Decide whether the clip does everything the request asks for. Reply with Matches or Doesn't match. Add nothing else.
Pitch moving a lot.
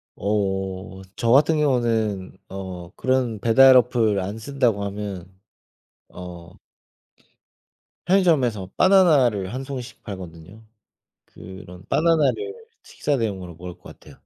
Matches